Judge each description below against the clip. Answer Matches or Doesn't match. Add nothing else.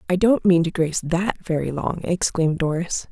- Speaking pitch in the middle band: Matches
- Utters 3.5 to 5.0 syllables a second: Doesn't match